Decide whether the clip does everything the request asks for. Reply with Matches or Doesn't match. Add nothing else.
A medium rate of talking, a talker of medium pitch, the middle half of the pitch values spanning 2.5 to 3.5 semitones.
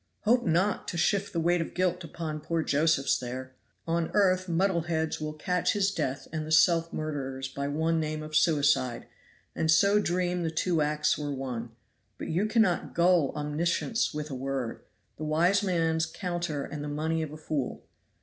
Matches